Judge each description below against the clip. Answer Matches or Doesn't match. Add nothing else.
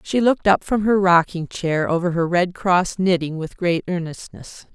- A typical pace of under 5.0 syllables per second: Matches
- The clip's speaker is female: Matches